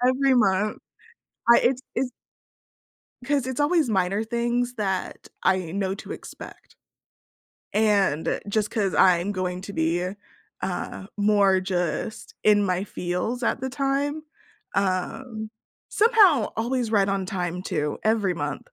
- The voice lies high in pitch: Yes, high, 205 Hz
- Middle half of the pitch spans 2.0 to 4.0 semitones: No, average, 4.8 semitones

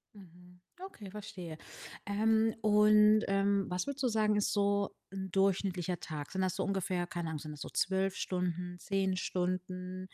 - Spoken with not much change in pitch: Yes, narrow, 2.2 semitones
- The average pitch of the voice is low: No, high, 190 Hz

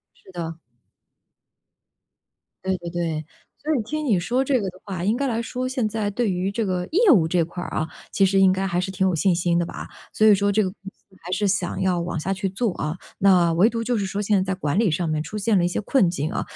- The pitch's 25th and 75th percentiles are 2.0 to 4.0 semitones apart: Yes, average, 3.7 semitones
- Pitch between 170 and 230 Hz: Yes, high, 190 Hz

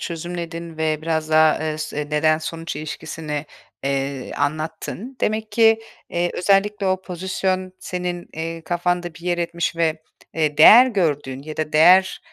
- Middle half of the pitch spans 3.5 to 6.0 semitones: No, average, 2.7 semitones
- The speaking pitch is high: No, medium, 165 Hz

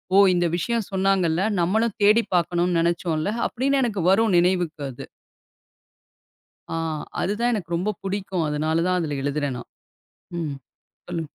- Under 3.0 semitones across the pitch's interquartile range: No, average, 3.7 semitones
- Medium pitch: Yes, medium, 180 Hz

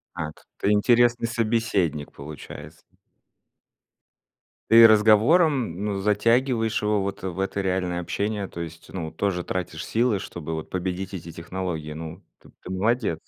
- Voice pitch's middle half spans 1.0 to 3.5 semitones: No, average, 4.6 semitones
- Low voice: Yes, very low, 95 Hz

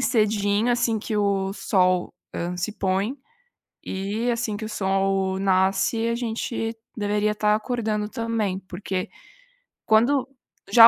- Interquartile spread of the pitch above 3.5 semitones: No, average, 2.8 semitones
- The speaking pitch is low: No, high, 210 Hz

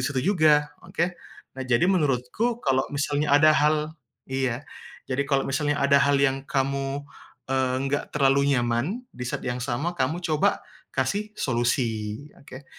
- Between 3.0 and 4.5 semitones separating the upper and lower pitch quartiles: No, narrow, 2.5 semitones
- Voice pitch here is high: No, medium, 140 Hz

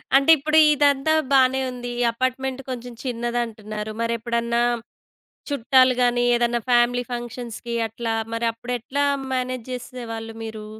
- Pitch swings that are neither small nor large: No, narrow, 1.8 semitones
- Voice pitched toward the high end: Yes, high, 240 Hz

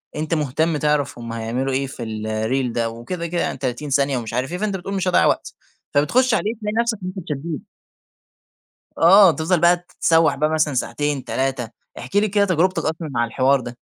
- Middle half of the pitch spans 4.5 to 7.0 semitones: Yes, wide, 5.6 semitones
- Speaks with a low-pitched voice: No, medium, 150 Hz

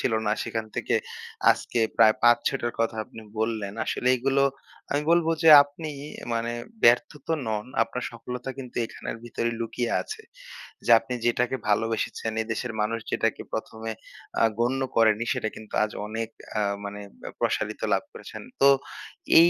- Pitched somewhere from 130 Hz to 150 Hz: No, low, 115 Hz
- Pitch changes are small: Yes, narrow, 2.1 semitones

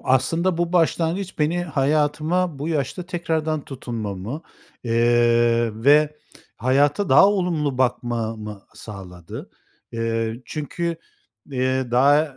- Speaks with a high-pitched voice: No, medium, 140 Hz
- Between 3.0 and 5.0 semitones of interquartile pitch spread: No, wide, 5.5 semitones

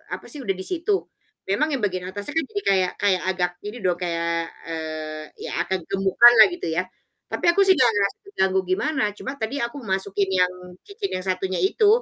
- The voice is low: No, high, 195 Hz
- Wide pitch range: Yes, wide, 7.6 semitones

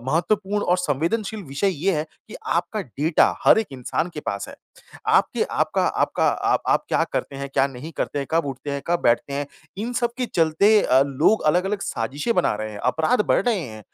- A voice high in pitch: No, medium, 160 Hz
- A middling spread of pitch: No, wide, 6.6 semitones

